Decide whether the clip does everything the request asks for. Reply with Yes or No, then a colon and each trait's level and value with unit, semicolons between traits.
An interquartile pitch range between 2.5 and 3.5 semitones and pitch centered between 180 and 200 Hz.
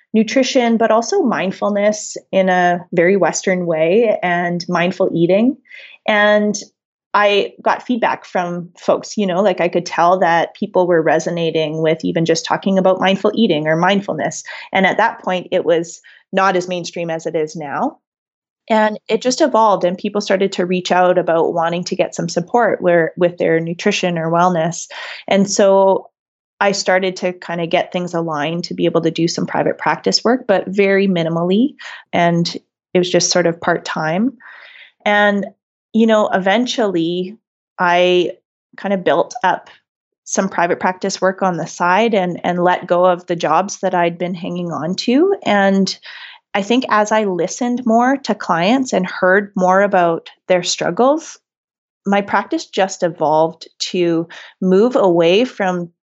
Yes: average, 3.1 semitones; medium, 185 Hz